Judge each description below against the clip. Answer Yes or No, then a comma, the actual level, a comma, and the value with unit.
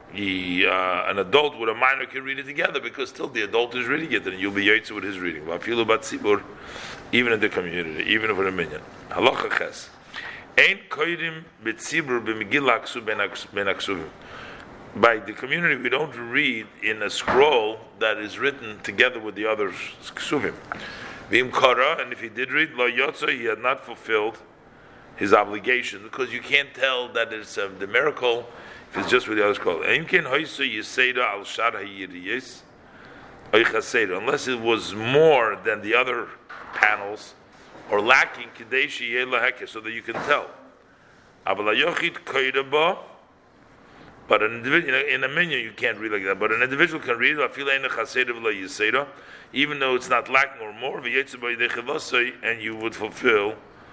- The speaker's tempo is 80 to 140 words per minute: Yes, slow, 135 wpm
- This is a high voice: No, low, 120 Hz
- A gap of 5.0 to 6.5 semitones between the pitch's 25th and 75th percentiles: No, average, 3.7 semitones